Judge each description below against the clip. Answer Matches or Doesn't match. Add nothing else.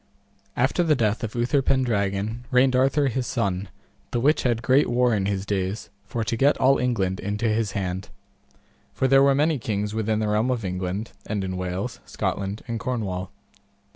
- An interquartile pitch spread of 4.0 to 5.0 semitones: Matches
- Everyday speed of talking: Matches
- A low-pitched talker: Matches